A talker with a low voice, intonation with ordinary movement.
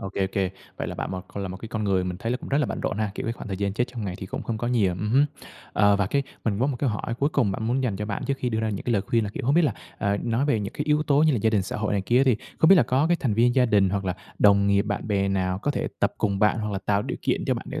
Yes: low, 110 Hz; average, 3.9 semitones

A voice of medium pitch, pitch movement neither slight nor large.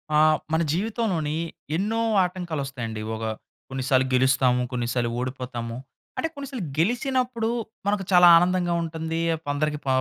No: medium, 160 Hz; wide, 6.9 semitones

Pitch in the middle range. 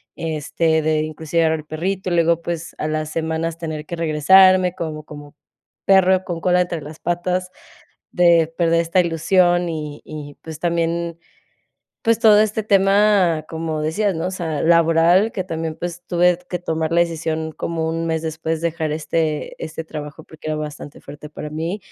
Yes: medium, 165 Hz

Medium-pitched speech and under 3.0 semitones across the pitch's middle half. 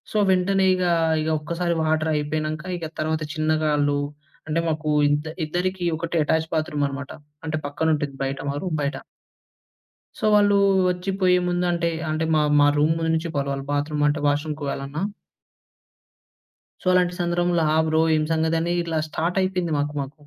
Yes: medium, 160 Hz; narrow, 2.6 semitones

